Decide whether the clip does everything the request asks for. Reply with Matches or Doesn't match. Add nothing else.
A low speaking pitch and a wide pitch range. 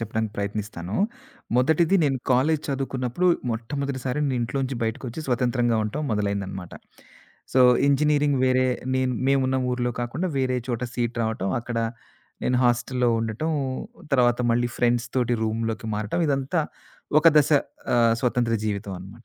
Doesn't match